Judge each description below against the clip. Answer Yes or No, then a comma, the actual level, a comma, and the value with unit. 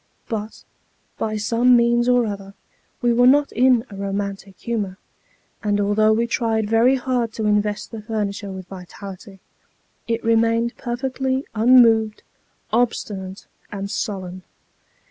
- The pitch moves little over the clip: No, average, 3.0 semitones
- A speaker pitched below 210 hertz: No, high, 220 Hz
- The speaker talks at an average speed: No, slow, 125 wpm